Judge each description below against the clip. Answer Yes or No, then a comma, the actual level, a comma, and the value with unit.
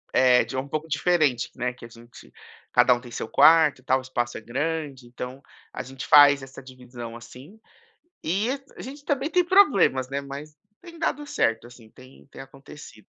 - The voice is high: No, low, 135 Hz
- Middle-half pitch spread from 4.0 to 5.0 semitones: Yes, average, 4.3 semitones